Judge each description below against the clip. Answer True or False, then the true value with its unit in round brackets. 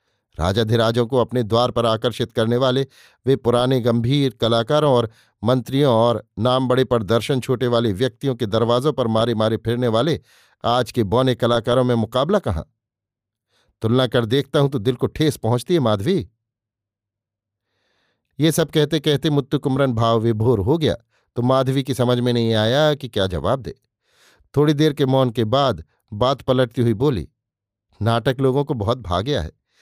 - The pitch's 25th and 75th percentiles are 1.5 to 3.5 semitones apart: True (2.7 semitones)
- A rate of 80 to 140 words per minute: False (165 wpm)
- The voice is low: True (120 Hz)